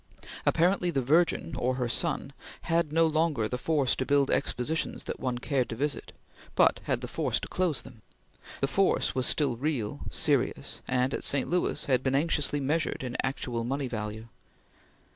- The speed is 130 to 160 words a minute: No, average, 175 wpm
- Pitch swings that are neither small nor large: Yes, average, 3.9 semitones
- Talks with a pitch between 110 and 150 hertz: Yes, low, 135 Hz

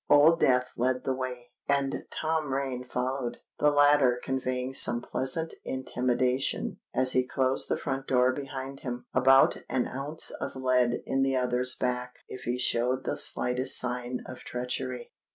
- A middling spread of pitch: No, narrow, 1.2 semitones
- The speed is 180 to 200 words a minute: No, average, 155 wpm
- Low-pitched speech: Yes, low, 130 Hz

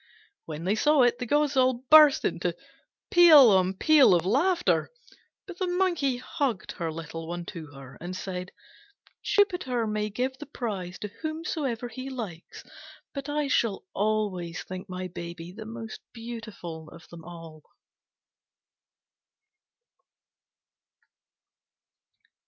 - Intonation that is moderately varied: No, wide, 7.7 semitones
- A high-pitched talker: Yes, high, 220 Hz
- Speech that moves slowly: Yes, slow, 125 wpm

